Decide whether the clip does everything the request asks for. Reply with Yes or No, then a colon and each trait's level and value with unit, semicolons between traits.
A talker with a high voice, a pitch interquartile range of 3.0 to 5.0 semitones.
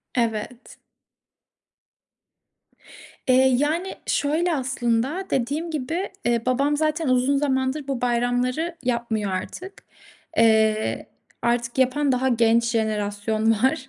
Yes: very high, 255 Hz; average, 3.9 semitones